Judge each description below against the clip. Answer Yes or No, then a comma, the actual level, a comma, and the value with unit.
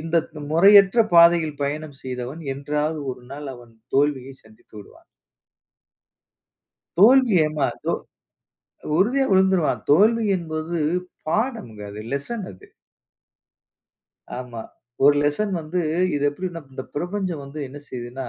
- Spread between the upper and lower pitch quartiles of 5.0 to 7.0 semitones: Yes, average, 5.3 semitones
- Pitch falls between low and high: Yes, medium, 155 Hz